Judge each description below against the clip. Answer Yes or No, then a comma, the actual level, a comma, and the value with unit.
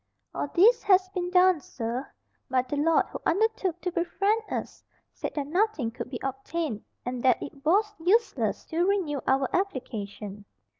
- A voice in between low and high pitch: No, very high, 325 Hz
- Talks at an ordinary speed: Yes, average, 160 wpm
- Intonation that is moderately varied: No, wide, 6.5 semitones